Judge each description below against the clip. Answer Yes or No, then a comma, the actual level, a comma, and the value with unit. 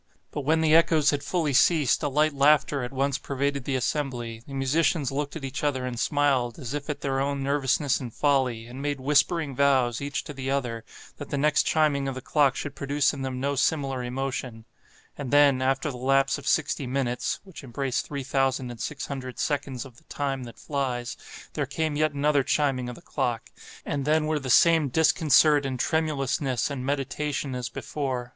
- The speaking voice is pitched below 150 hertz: Yes, medium, 140 Hz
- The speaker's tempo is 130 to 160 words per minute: No, average, 200 wpm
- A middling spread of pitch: No, narrow, 2.1 semitones